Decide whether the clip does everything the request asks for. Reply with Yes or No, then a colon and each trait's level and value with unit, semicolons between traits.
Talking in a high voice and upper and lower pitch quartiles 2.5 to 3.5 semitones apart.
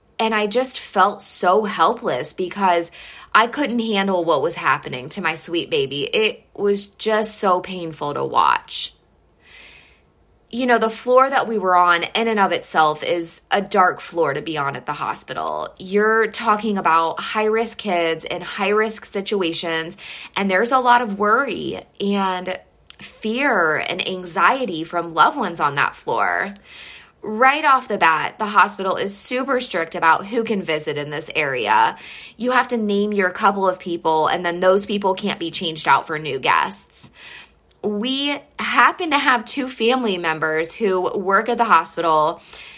No: high, 200 Hz; average, 5.1 semitones